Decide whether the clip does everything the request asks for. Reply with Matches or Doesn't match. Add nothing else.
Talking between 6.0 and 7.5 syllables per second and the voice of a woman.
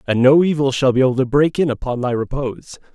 Doesn't match